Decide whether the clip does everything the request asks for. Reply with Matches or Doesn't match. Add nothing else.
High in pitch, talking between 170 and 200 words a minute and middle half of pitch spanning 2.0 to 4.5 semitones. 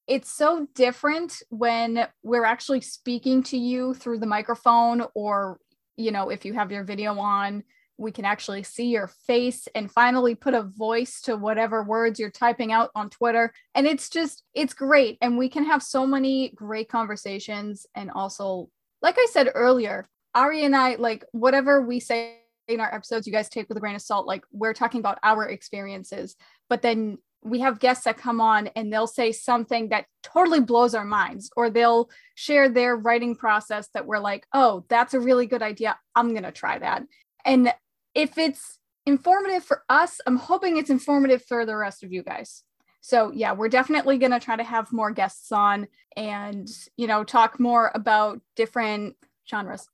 Matches